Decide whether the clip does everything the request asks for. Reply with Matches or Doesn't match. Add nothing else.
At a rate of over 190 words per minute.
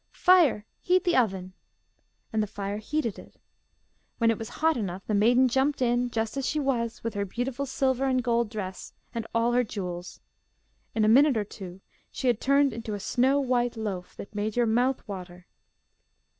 Doesn't match